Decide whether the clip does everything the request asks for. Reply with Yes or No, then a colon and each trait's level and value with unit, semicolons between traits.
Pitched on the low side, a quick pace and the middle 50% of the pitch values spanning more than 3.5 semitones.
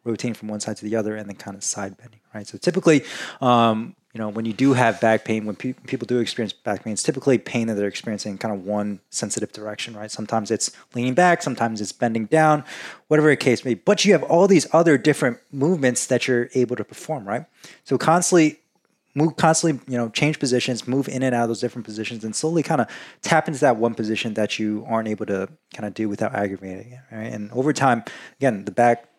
Yes: low, 120 Hz; fast, 235 wpm; average, 4.3 semitones